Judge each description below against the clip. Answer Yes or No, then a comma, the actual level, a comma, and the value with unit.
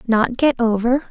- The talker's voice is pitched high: Yes, high, 240 Hz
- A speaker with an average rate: Yes, average, 165 wpm